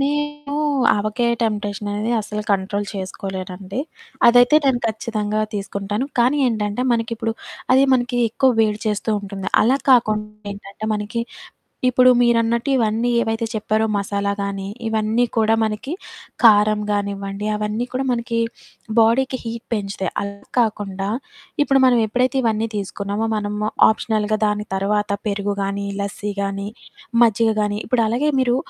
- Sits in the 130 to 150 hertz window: No, high, 215 Hz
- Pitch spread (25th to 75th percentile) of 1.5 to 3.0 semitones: Yes, narrow, 2.6 semitones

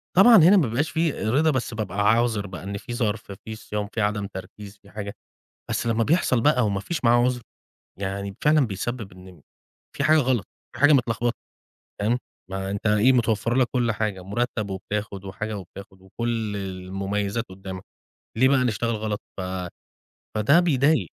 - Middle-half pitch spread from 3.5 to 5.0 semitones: Yes, average, 3.8 semitones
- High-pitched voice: No, low, 110 Hz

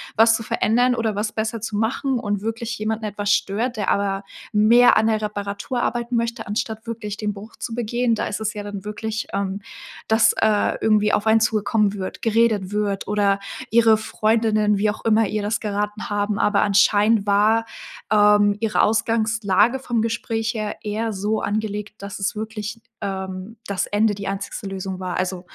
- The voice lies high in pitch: Yes, high, 215 Hz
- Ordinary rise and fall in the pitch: No, narrow, 1.6 semitones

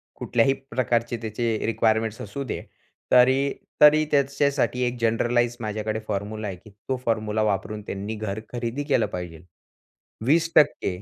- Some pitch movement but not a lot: Yes, average, 3.3 semitones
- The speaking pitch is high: No, low, 115 Hz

